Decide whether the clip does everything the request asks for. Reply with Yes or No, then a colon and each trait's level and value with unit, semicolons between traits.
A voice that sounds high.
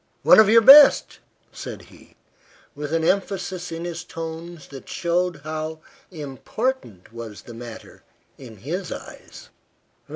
No: medium, 165 Hz